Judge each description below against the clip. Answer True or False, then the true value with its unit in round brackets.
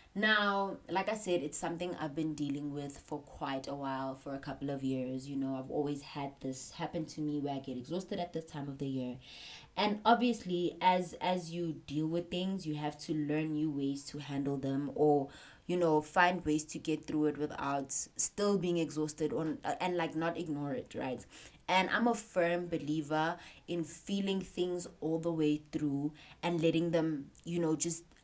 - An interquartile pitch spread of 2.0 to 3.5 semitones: True (3.2 semitones)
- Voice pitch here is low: False (155 Hz)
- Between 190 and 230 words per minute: True (200 wpm)